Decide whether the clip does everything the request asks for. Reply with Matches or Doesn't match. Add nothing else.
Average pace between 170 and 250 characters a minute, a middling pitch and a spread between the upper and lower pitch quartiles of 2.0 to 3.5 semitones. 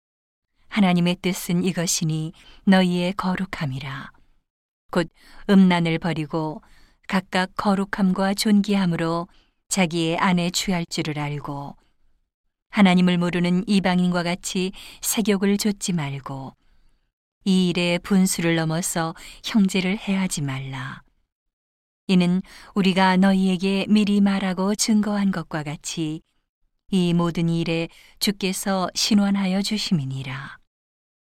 Matches